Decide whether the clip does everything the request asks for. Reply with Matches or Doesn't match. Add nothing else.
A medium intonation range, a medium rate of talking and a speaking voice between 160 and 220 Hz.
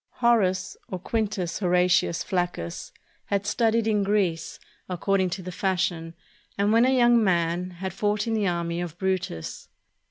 Matches